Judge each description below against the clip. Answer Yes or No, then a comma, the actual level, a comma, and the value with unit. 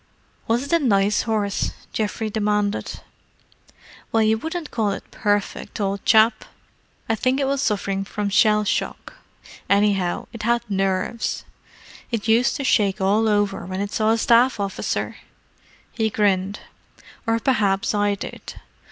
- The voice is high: Yes, high, 210 Hz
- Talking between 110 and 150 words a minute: Yes, average, 145 wpm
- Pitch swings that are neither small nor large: No, narrow, 2.2 semitones